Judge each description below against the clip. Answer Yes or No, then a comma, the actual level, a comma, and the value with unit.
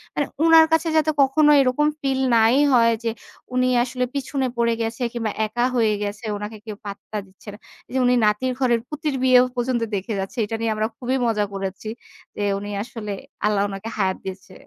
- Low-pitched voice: No, high, 230 Hz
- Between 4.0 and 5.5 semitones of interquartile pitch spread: No, average, 3.6 semitones